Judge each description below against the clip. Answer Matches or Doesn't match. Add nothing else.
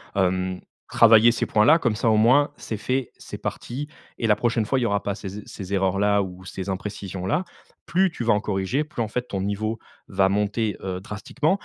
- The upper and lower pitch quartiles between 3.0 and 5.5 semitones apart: Matches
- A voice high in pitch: Doesn't match